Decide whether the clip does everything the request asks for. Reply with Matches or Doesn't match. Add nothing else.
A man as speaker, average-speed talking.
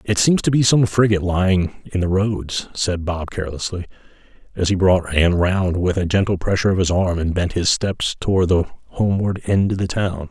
Doesn't match